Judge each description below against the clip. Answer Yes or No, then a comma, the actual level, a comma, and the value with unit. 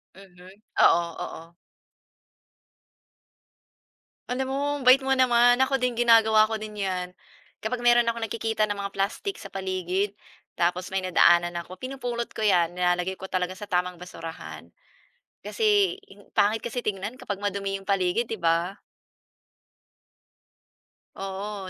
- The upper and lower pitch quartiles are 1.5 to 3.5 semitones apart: No, average, 4.4 semitones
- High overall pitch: Yes, high, 200 Hz